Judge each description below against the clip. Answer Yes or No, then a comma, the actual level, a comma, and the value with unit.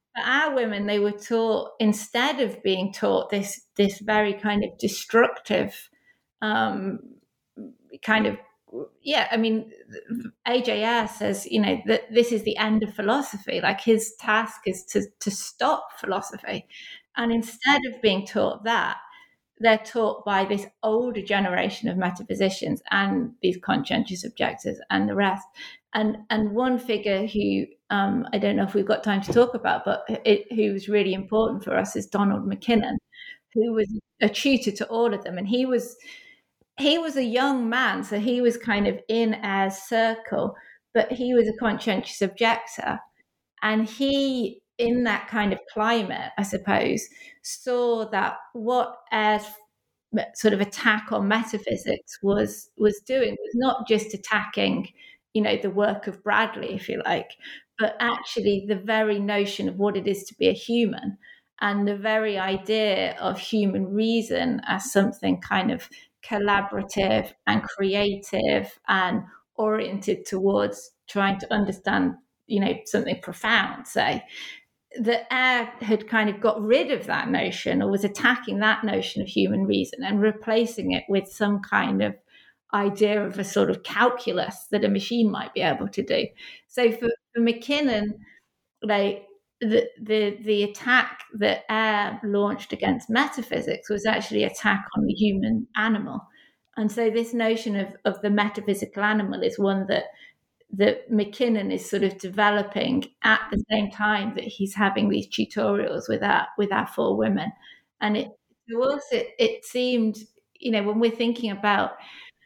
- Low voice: No, high, 220 Hz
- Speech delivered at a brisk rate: No, average, 160 wpm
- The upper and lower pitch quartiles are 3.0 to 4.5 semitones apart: No, narrow, 2.6 semitones